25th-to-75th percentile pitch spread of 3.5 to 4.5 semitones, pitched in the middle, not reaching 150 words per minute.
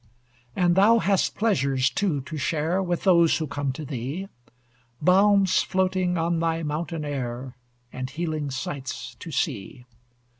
No: average, 5.2 semitones; medium, 160 Hz; average, 140 wpm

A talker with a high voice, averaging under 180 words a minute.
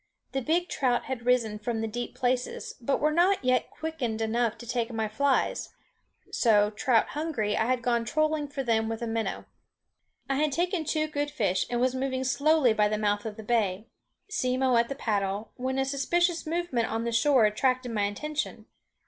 No: high, 245 Hz; average, 190 wpm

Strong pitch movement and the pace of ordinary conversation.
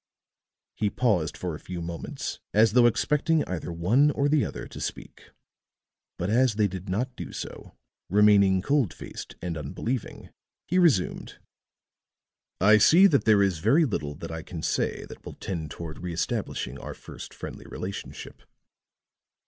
Yes: wide, 6.7 semitones; average, 155 wpm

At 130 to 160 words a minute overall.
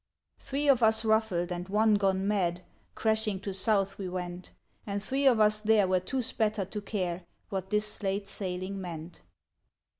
No: average, 170 wpm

